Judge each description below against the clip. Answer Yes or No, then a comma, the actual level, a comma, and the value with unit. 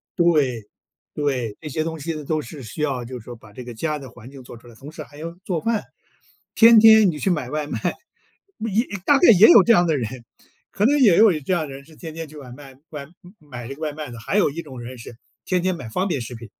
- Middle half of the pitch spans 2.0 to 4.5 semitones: No, wide, 5.5 semitones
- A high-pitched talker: No, medium, 150 Hz